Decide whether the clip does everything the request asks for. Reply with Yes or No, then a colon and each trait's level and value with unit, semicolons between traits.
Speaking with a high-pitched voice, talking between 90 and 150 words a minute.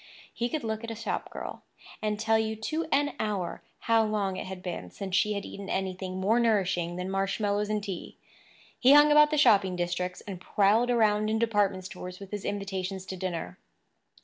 No: high, 205 Hz; average, 195 wpm